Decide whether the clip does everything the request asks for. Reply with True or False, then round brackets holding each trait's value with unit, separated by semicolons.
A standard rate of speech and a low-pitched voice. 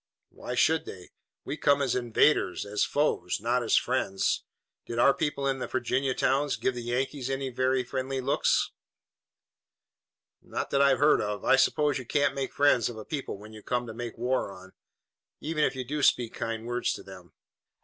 True (190 wpm; 130 Hz)